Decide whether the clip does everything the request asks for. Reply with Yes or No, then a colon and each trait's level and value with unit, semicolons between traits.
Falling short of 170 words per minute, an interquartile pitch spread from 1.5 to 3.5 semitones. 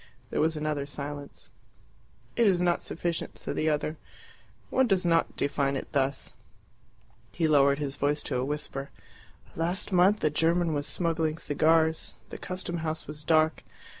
Yes: average, 155 wpm; average, 2.8 semitones